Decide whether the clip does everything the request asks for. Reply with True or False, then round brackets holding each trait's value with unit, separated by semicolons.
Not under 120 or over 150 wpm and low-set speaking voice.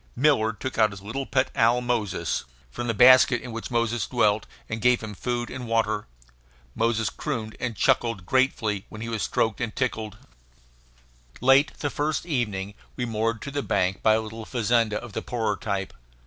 False (180 wpm; 115 Hz)